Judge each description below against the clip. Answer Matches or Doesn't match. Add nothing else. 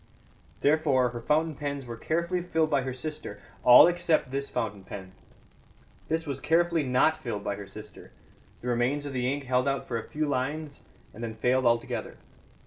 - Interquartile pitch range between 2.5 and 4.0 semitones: Doesn't match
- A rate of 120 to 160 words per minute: Doesn't match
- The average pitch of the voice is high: Doesn't match